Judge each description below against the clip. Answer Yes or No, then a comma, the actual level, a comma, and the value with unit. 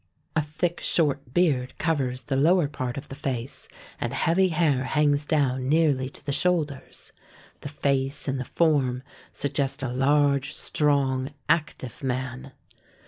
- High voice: No, medium, 140 Hz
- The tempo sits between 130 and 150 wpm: Yes, average, 140 wpm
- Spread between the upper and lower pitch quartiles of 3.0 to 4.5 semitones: No, narrow, 2.6 semitones